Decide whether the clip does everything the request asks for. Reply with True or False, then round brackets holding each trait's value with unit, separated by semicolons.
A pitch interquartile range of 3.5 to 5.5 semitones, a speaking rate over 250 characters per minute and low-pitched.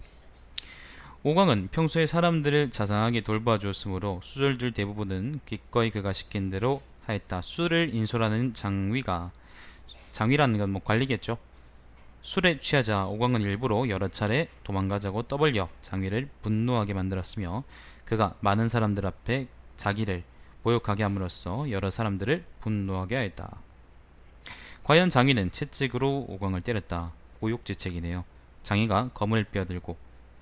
True (5.1 semitones; 310 characters per minute; 105 Hz)